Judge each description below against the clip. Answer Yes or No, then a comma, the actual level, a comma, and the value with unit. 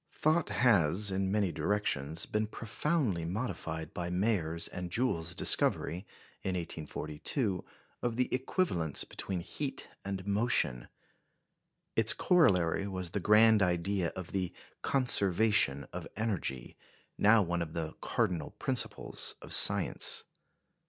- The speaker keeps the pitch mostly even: No, average, 4.5 semitones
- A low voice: Yes, very low, 95 Hz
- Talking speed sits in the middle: No, slow, 120 wpm